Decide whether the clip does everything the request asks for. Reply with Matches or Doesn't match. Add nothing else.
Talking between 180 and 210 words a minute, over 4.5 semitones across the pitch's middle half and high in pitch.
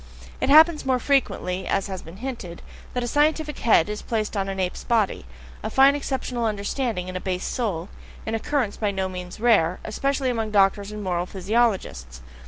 Matches